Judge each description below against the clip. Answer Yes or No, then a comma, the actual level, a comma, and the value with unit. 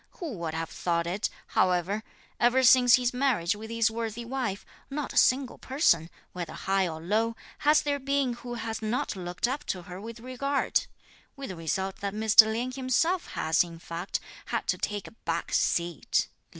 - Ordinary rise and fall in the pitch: No, wide, 6.2 semitones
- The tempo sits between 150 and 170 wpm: No, average, 185 wpm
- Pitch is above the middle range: Yes, high, 220 Hz